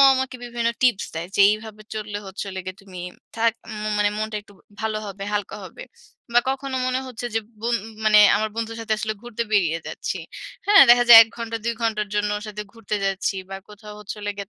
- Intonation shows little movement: Yes, narrow, 2.1 semitones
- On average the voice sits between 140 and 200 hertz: No, high, 215 Hz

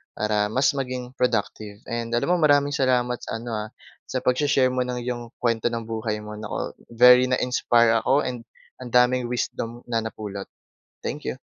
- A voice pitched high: No, low, 120 Hz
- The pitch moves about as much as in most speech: No, narrow, 2.0 semitones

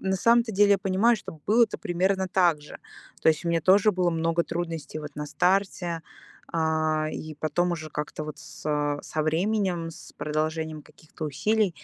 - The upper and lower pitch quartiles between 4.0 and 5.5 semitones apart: No, average, 3.5 semitones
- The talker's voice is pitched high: No, medium, 170 Hz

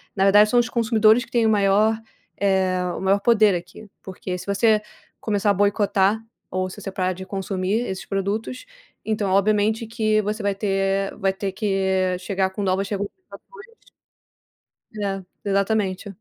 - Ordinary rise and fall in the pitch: No, narrow, 2.0 semitones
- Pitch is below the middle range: No, high, 200 Hz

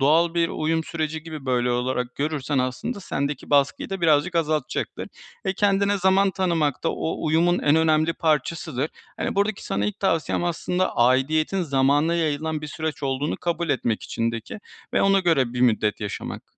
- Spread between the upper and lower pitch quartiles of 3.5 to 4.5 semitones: Yes, average, 4.1 semitones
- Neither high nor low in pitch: Yes, medium, 155 Hz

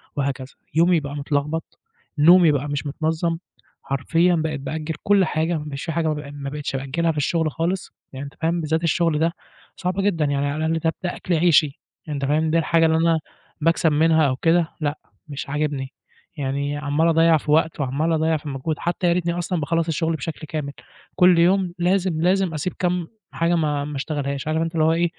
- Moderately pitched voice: Yes, medium, 160 Hz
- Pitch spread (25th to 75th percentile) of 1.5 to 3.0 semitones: Yes, narrow, 2.4 semitones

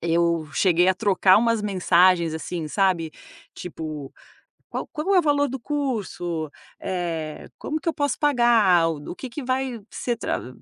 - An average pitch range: No, wide, 7.2 semitones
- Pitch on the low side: No, medium, 185 Hz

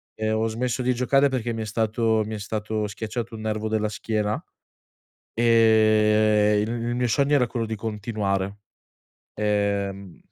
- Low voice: Yes, low, 110 Hz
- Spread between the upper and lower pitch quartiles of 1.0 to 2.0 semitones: Yes, narrow, 1.5 semitones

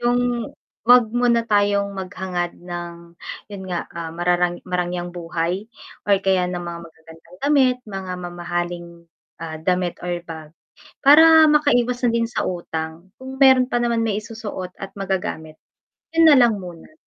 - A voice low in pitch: No, medium, 185 Hz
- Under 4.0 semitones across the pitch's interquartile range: No, average, 5.3 semitones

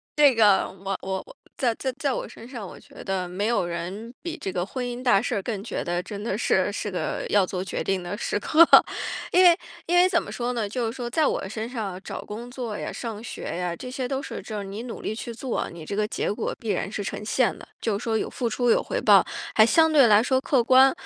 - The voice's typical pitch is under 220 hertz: No, high, 225 Hz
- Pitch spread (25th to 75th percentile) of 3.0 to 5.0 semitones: Yes, average, 4.1 semitones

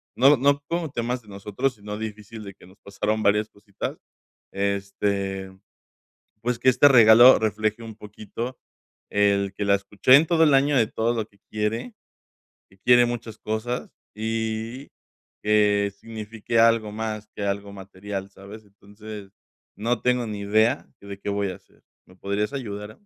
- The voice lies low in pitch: Yes, low, 110 Hz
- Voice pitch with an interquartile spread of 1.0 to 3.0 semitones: Yes, narrow, 2.6 semitones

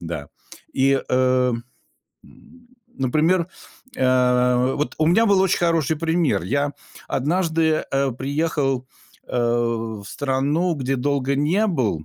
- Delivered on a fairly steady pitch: No, average, 4.2 semitones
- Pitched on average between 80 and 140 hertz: Yes, low, 135 Hz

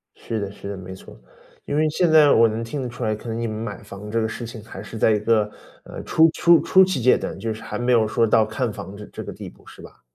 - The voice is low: Yes, low, 115 Hz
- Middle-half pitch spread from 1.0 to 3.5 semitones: Yes, average, 2.9 semitones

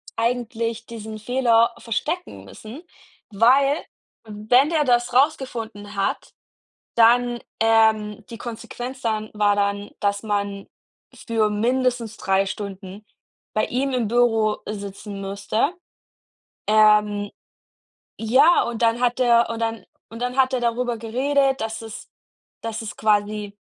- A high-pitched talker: Yes, high, 225 Hz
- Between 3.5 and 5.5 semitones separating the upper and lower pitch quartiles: No, narrow, 2.6 semitones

